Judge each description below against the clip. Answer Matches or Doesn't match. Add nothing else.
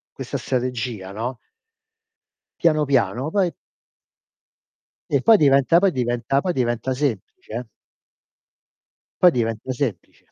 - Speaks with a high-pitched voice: Doesn't match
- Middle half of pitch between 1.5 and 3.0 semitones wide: Doesn't match